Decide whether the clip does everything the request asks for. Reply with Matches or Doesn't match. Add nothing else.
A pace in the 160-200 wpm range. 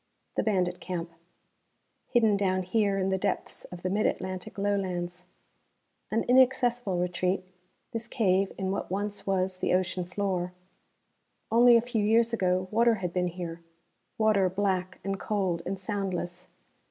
Doesn't match